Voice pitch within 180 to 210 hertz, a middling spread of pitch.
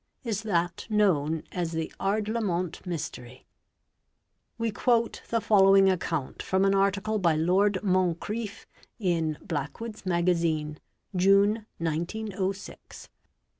Yes: high, 190 Hz; average, 3.9 semitones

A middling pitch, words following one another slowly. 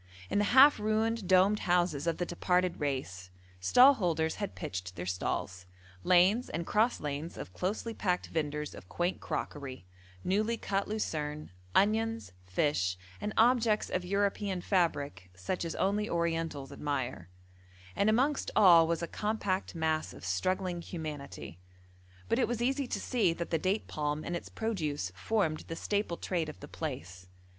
No: medium, 175 Hz; average, 155 wpm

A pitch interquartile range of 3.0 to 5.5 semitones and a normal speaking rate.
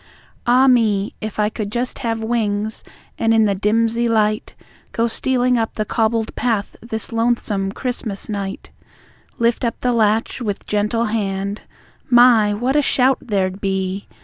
No: narrow, 2.5 semitones; average, 150 wpm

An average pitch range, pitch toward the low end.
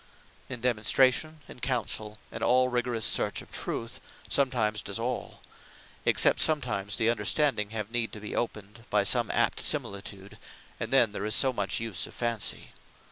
Yes: average, 3.0 semitones; low, 115 Hz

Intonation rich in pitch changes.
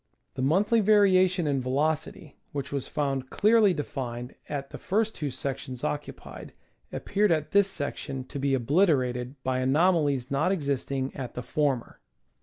Yes: wide, 5.7 semitones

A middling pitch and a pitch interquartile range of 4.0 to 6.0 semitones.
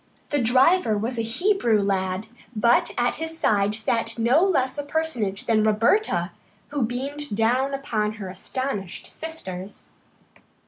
No: high, 235 Hz; average, 5.1 semitones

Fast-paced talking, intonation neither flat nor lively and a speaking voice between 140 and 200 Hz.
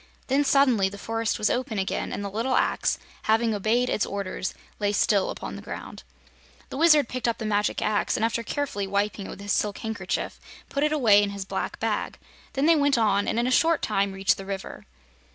No: fast, 215 wpm; average, 4.1 semitones; high, 220 Hz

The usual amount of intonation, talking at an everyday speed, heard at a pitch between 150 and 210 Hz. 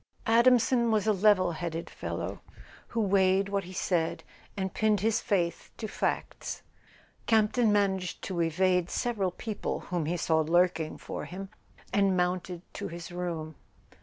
Yes: average, 3.2 semitones; average, 145 wpm; medium, 185 Hz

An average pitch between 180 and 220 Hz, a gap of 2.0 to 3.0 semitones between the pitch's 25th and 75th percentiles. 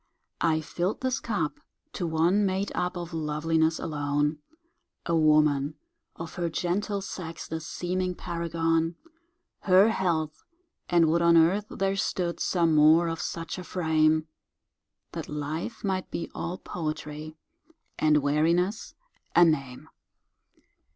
No: medium, 165 Hz; narrow, 2.6 semitones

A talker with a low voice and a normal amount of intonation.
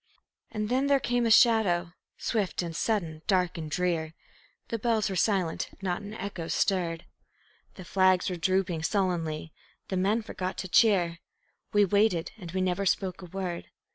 No: medium, 185 Hz; average, 3.3 semitones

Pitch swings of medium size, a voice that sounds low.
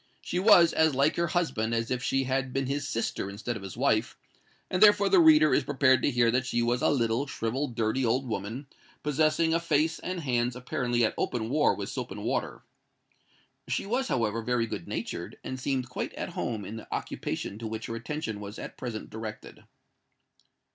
Yes: average, 4.5 semitones; low, 125 Hz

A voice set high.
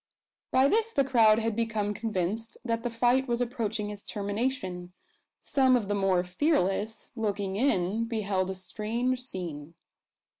Yes: high, 220 Hz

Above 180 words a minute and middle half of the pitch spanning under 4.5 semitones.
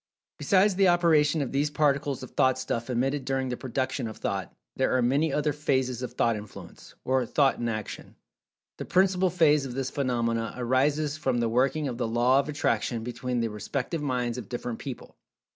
Yes: average, 190 wpm; average, 3.4 semitones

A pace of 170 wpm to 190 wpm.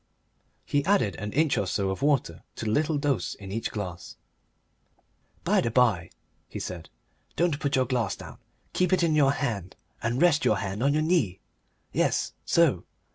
Yes: average, 180 wpm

